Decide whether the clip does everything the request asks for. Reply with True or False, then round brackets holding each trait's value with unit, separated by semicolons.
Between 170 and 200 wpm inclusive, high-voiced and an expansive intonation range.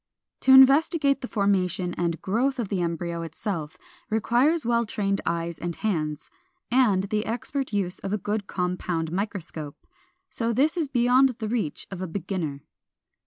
False (155 wpm; 200 Hz; 5.8 semitones)